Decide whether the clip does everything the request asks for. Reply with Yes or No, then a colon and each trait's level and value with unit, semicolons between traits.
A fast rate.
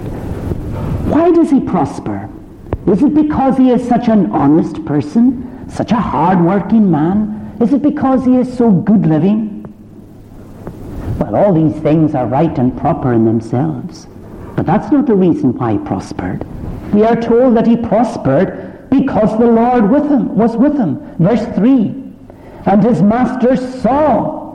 No: average, 155 wpm